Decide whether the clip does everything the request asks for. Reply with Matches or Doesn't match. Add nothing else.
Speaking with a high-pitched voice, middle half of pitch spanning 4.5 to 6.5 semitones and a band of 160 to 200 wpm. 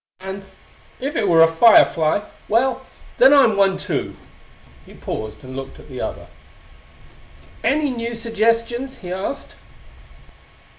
Doesn't match